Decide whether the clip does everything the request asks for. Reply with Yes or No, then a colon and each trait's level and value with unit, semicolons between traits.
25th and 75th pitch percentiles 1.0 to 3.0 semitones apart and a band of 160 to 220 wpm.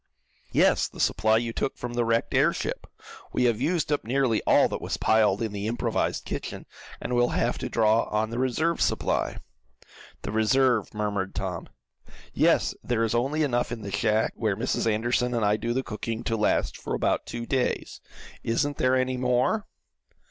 Yes: narrow, 2.5 semitones; average, 180 wpm